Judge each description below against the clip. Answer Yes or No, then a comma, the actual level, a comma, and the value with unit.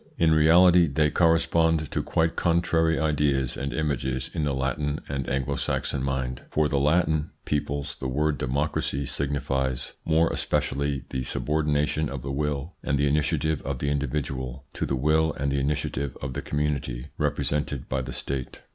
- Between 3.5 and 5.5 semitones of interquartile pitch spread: No, narrow, 2.4 semitones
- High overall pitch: No, very low, 70 Hz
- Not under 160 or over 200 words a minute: Yes, average, 165 wpm